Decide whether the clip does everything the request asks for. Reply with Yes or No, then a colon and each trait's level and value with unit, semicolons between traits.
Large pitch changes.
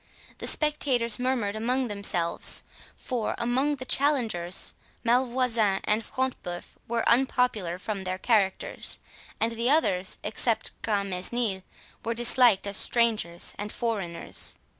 No: average, 4.0 semitones